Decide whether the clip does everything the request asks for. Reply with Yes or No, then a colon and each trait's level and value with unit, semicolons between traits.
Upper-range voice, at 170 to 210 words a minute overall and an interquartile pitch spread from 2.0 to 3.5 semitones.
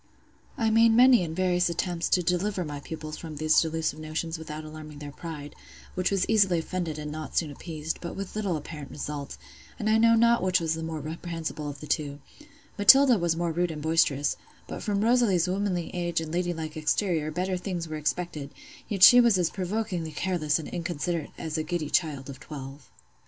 No: medium, 165 Hz; average, 190 wpm; average, 3.1 semitones